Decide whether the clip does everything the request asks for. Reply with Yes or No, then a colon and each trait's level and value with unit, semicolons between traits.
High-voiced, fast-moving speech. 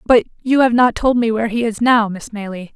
Yes: high, 230 Hz; fast, 260 wpm